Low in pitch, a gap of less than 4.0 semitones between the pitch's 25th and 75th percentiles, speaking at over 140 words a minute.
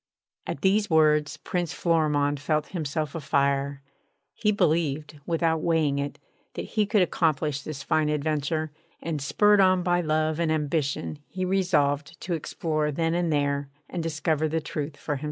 No: medium, 155 Hz; narrow, 2.6 semitones; average, 160 wpm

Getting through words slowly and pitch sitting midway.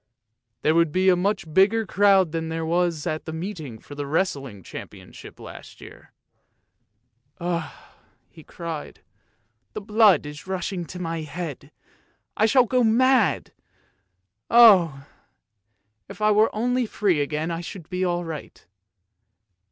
No: average, 145 wpm; medium, 175 Hz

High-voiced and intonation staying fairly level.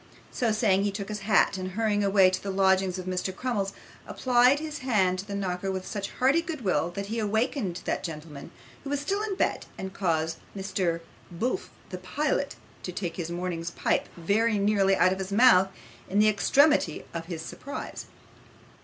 No: high, 195 Hz; average, 3.7 semitones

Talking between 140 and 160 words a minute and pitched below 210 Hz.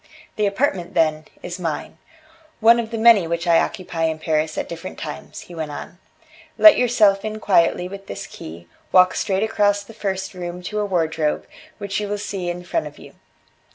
No: average, 190 wpm; medium, 185 Hz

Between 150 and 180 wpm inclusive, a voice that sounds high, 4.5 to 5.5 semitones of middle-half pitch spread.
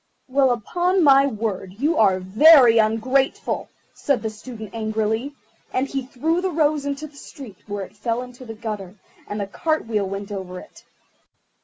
Yes: average, 170 wpm; high, 230 Hz; average, 4.9 semitones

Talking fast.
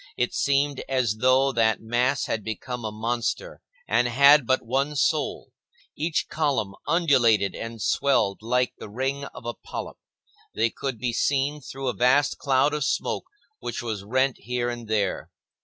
No: average, 160 wpm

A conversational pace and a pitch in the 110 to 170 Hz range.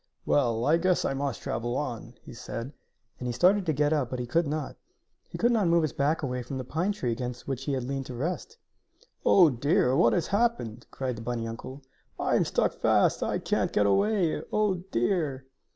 No: fast, 215 wpm; low, 135 Hz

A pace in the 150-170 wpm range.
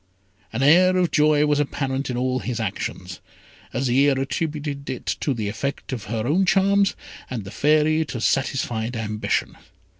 Yes: average, 155 wpm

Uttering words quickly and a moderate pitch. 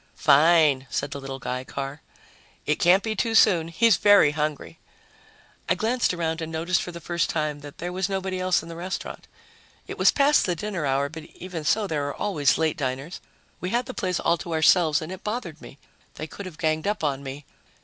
Yes: fast, 210 wpm; medium, 165 Hz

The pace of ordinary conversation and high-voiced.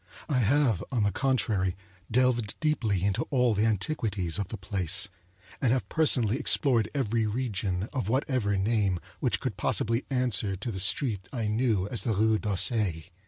No: average, 165 wpm; low, 110 Hz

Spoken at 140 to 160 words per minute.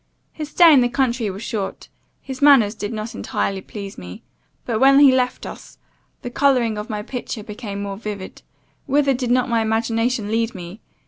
No: average, 185 wpm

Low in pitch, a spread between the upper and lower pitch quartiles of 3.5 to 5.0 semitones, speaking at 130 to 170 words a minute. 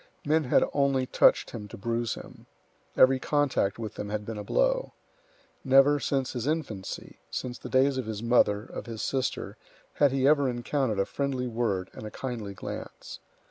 No: low, 125 Hz; average, 4.1 semitones; average, 180 wpm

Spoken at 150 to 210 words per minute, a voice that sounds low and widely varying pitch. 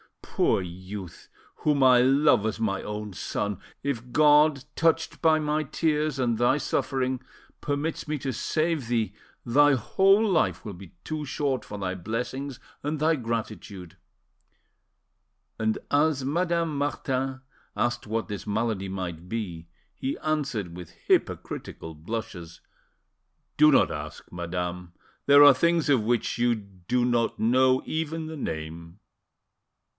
No: slow, 135 wpm; low, 125 Hz; wide, 6.7 semitones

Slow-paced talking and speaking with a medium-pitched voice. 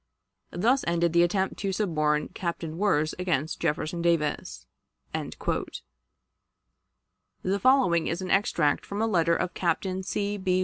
Yes: slow, 130 wpm; medium, 175 Hz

